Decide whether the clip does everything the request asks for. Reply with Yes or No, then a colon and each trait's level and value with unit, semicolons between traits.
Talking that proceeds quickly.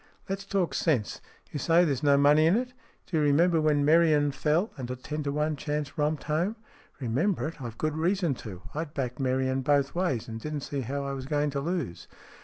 Yes: fast, 220 wpm